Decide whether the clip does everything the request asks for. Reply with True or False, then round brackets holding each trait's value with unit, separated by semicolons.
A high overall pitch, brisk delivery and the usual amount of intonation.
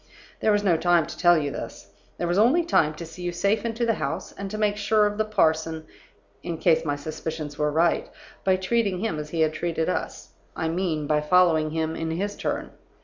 False (170 Hz; 220 wpm; 4.4 semitones)